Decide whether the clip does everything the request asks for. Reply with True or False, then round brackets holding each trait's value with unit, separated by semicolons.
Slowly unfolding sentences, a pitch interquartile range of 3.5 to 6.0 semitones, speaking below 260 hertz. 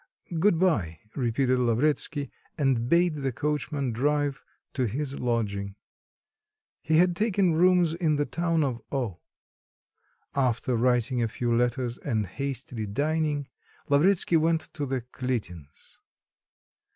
True (120 wpm; 4.7 semitones; 135 Hz)